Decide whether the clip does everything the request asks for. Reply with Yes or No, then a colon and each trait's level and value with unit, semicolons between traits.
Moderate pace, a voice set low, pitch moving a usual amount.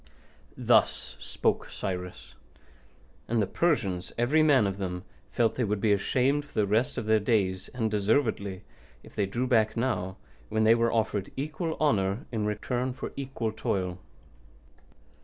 Yes: average, 155 wpm; low, 110 Hz; average, 4.3 semitones